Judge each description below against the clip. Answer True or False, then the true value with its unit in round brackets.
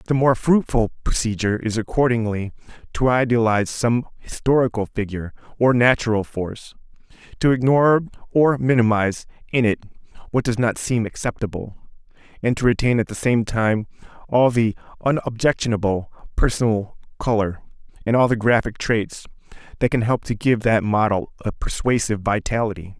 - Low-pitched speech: True (115 Hz)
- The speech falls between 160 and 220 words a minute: False (135 wpm)